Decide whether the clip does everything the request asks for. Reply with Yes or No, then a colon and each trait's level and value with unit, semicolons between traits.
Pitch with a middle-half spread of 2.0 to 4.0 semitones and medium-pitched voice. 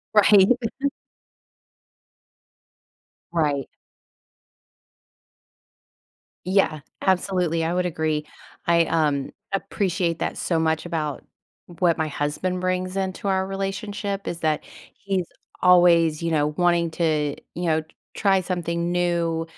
Yes: average, 2.9 semitones; medium, 175 Hz